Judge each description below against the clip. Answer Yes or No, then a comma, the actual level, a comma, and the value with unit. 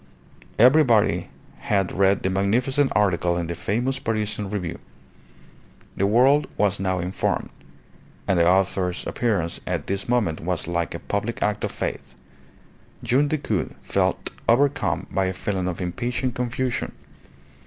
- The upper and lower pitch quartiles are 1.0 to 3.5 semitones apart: No, average, 4.9 semitones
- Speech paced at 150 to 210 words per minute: No, slow, 135 wpm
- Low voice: Yes, low, 100 Hz